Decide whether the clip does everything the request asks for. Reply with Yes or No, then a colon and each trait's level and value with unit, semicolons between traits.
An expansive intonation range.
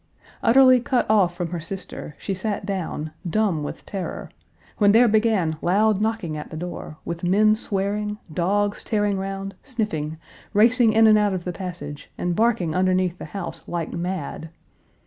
No: average, 3.7 semitones